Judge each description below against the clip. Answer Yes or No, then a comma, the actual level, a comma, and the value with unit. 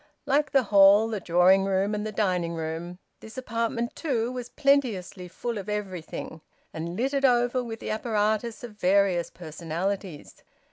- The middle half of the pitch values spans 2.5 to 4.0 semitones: No, average, 4.8 semitones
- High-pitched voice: Yes, high, 210 Hz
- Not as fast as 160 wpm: Yes, average, 150 wpm